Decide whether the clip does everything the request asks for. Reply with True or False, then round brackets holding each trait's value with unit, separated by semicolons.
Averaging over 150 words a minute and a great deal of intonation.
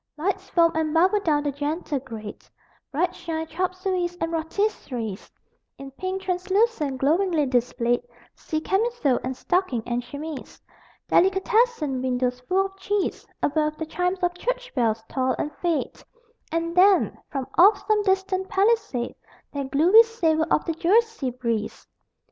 False (140 wpm; 5.9 semitones)